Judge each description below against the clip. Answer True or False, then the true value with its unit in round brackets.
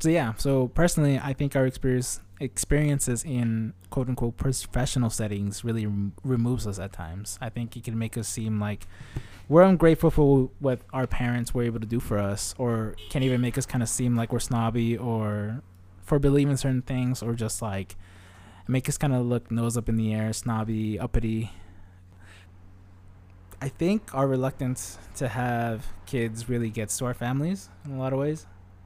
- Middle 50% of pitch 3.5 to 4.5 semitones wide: True (4.1 semitones)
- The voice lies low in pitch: True (120 Hz)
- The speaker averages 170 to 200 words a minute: True (185 wpm)